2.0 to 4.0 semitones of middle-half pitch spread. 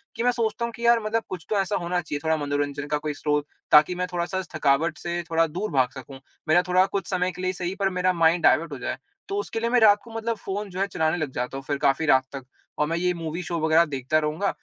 No: average, 4.4 semitones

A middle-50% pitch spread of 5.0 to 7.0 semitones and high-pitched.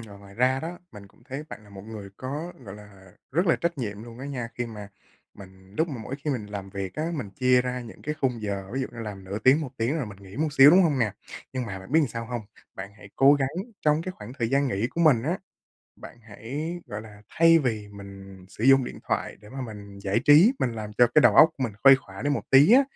No: wide, 5.6 semitones; low, 120 Hz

